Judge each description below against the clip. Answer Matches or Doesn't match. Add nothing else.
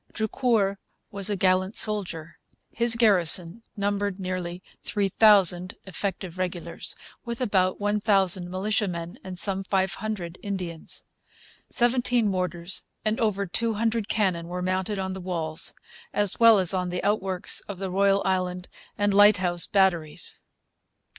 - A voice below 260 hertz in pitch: Matches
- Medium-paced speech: Doesn't match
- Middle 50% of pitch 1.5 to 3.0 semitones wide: Matches